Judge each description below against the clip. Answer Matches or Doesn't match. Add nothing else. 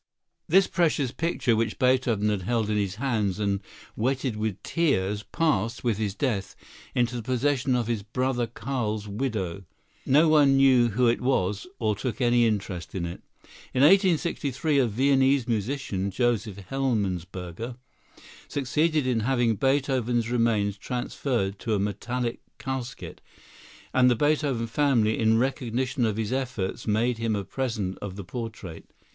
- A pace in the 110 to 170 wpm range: Matches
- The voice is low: Matches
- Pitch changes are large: Doesn't match